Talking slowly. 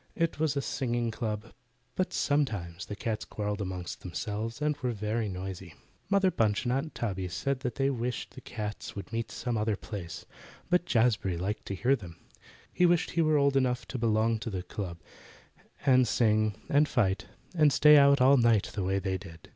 No: average, 185 wpm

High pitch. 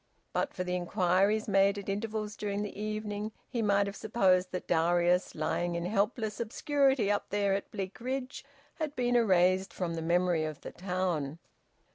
Yes: high, 200 Hz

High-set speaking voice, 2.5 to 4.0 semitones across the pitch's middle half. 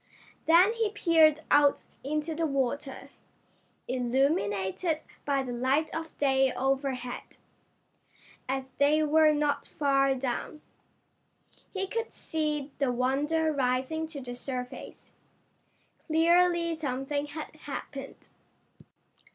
Yes: very high, 285 Hz; average, 3.2 semitones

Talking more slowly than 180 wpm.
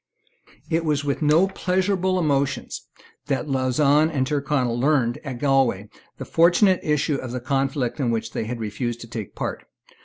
Yes: average, 165 wpm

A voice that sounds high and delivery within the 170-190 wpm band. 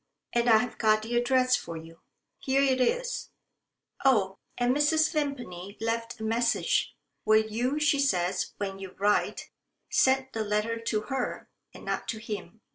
No: high, 230 Hz; average, 155 wpm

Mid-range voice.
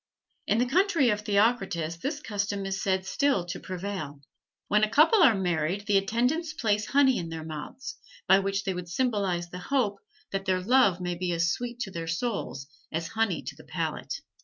No: high, 200 Hz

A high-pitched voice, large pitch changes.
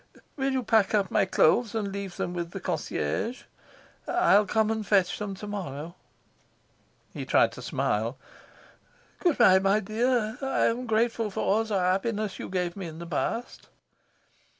No: high, 205 Hz; average, 3.3 semitones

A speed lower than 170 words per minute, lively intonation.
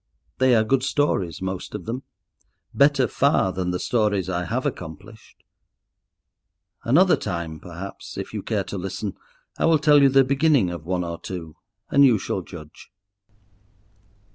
Yes: average, 155 wpm; wide, 7.3 semitones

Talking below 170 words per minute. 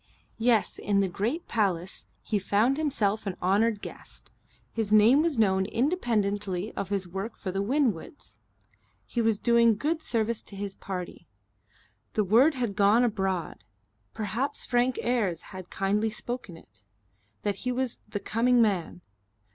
Yes: average, 145 wpm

